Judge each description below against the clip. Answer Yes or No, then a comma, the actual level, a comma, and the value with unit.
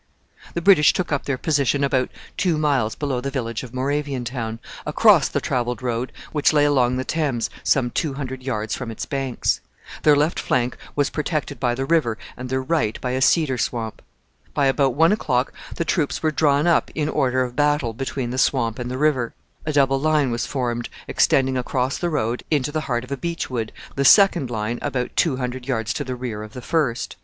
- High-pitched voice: No, low, 130 Hz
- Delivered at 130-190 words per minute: No, fast, 205 wpm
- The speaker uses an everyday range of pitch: Yes, average, 3.1 semitones